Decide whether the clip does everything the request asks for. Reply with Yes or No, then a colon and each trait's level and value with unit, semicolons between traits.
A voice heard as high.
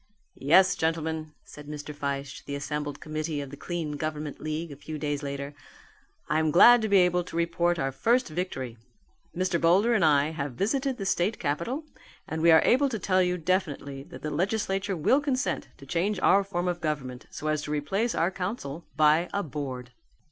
No: medium, 160 Hz